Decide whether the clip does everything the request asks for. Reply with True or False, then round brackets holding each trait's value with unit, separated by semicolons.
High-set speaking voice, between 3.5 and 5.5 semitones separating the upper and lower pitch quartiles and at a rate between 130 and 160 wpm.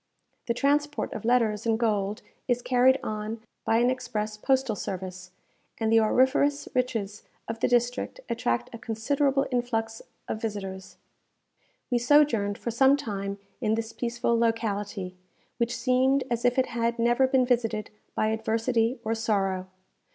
False (230 Hz; 2.7 semitones; 145 wpm)